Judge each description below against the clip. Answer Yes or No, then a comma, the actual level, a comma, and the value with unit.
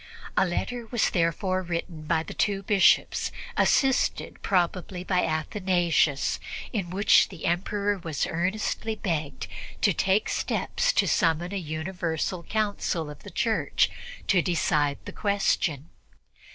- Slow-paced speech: Yes, slow, 125 wpm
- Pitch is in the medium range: Yes, medium, 180 Hz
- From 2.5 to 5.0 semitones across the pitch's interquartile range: Yes, average, 3.6 semitones